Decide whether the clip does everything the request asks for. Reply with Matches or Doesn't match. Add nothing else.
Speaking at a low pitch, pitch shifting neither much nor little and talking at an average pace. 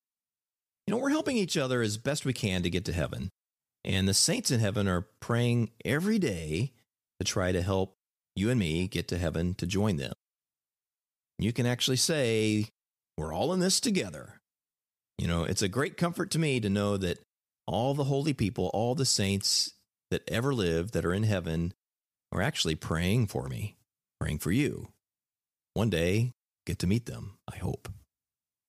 Doesn't match